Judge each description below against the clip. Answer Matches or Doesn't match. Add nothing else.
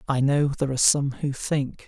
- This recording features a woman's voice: Doesn't match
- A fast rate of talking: Matches